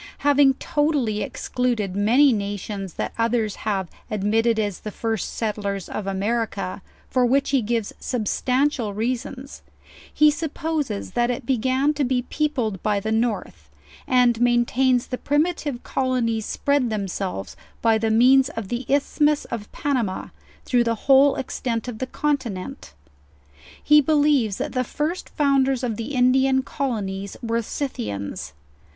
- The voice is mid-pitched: No, high, 240 Hz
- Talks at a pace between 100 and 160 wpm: Yes, average, 145 wpm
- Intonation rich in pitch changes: No, average, 4.1 semitones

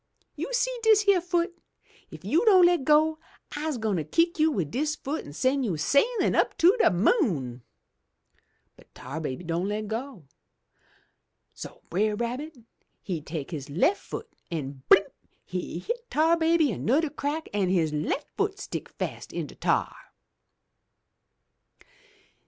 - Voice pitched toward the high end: Yes, very high, 270 Hz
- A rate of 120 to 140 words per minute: No, average, 150 wpm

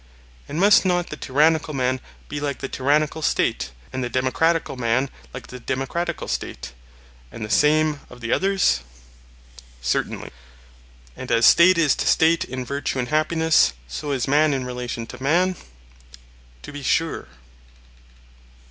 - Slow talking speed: No, average, 150 wpm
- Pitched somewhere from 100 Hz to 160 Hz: Yes, medium, 140 Hz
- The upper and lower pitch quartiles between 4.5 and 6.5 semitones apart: No, average, 4.1 semitones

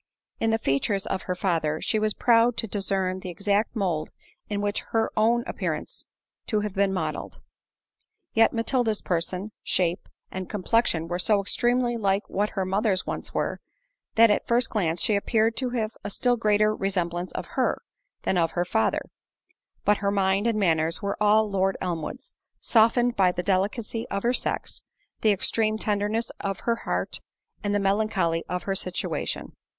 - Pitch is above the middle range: Yes, high, 205 Hz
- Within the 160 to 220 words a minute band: Yes, average, 170 wpm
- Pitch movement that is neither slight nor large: Yes, average, 3.2 semitones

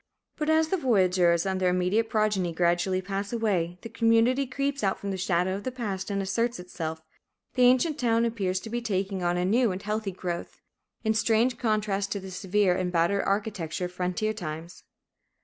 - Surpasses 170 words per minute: Yes, average, 190 wpm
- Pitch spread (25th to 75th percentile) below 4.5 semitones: Yes, average, 4.0 semitones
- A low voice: No, high, 200 Hz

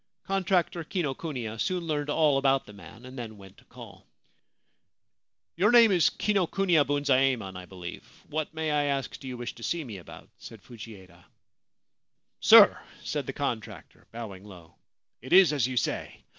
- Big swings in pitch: Yes, wide, 6.6 semitones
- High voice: No, low, 135 Hz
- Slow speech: No, average, 170 wpm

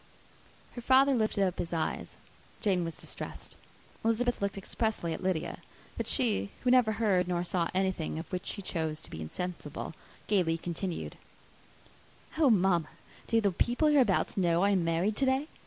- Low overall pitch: No, high, 190 Hz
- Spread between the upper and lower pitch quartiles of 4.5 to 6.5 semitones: Yes, average, 4.8 semitones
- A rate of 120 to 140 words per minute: No, average, 165 wpm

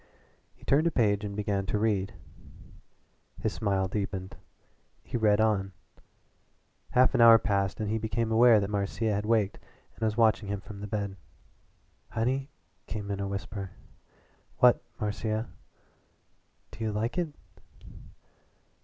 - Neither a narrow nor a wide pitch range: No, narrow, 2.0 semitones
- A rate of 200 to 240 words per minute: No, average, 140 wpm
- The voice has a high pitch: No, low, 105 Hz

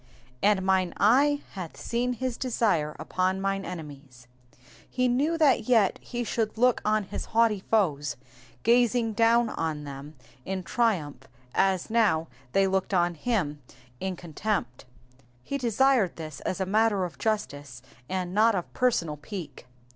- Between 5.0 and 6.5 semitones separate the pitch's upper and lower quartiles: Yes, wide, 5.5 semitones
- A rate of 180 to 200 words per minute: No, average, 145 wpm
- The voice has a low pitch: No, high, 195 Hz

